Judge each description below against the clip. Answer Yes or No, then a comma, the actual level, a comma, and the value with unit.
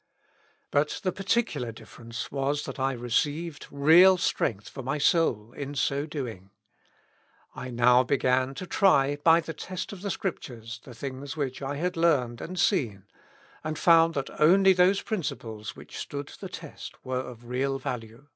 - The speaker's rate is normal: Yes, average, 165 wpm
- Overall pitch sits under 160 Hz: Yes, medium, 140 Hz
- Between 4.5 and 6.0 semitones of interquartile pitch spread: Yes, average, 5.0 semitones